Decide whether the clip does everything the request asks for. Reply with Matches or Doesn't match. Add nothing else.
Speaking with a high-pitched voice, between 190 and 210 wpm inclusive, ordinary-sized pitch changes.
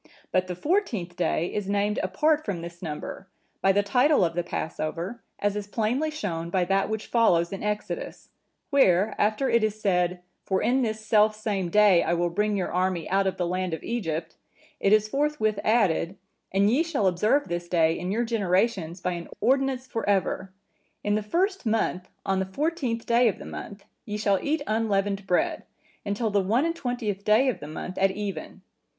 Matches